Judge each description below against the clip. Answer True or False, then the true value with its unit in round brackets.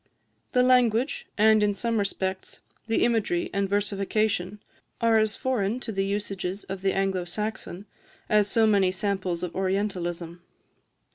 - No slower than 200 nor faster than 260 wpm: False (140 wpm)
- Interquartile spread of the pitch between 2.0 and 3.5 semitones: True (2.5 semitones)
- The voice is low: False (200 Hz)